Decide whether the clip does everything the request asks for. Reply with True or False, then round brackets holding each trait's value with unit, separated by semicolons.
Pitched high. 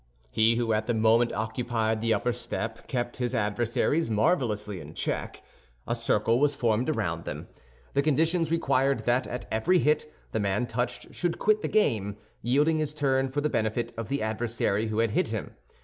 False (120 Hz)